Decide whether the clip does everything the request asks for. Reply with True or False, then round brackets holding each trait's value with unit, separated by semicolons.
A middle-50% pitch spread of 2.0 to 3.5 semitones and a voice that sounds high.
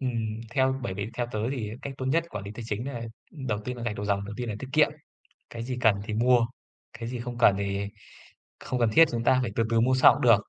False (3.0 semitones; 120 Hz)